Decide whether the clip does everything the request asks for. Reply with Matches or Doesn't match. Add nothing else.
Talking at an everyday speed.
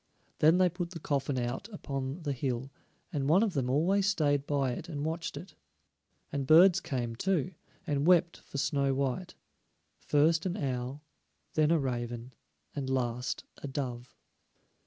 Matches